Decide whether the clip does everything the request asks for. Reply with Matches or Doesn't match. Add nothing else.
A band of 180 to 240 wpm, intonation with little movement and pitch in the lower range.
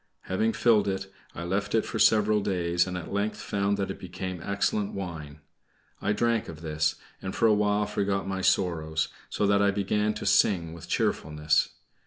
Doesn't match